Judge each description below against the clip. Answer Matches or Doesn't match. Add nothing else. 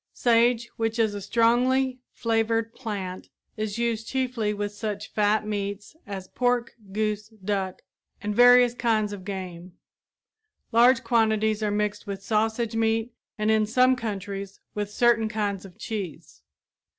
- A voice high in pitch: Matches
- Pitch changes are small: Matches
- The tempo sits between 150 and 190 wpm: Doesn't match